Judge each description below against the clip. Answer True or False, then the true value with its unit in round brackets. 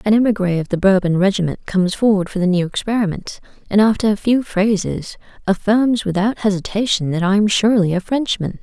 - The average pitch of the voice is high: True (200 Hz)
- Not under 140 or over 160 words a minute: False (180 wpm)